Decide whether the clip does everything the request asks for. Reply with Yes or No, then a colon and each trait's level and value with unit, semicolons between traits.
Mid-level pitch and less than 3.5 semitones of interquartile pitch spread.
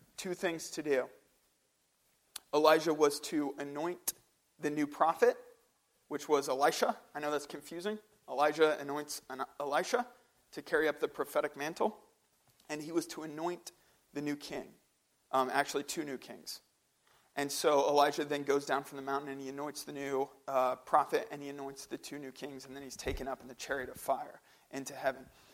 Yes: medium, 145 Hz; narrow, 2.6 semitones